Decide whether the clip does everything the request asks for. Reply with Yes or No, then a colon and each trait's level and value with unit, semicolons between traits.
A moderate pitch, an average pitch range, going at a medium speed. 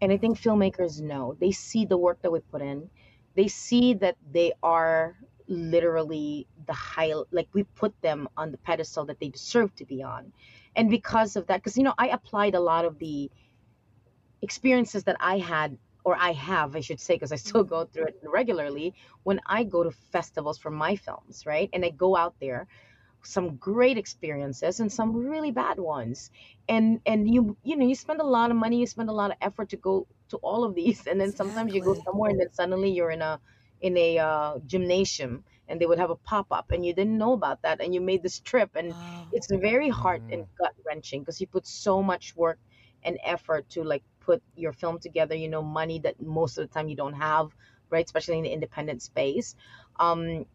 No: medium, 170 Hz; average, 4.5 semitones; fast, 215 wpm